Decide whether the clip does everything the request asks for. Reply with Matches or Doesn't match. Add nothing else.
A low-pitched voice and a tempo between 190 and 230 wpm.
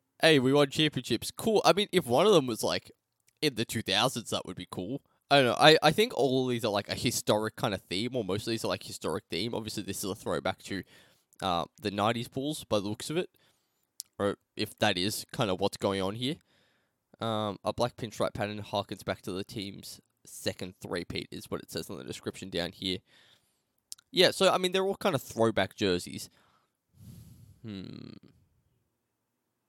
Matches